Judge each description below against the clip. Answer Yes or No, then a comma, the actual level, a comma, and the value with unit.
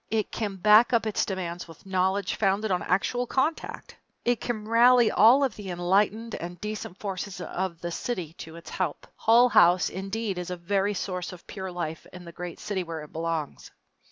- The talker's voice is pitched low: No, high, 190 Hz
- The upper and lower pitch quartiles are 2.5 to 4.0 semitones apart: Yes, average, 3.6 semitones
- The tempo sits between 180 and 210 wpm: Yes, average, 190 wpm